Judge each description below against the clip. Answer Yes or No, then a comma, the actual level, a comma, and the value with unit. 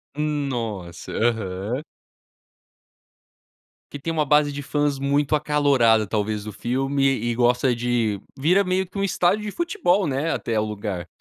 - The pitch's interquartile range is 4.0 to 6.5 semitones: Yes, average, 5.1 semitones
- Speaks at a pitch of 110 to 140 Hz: Yes, low, 135 Hz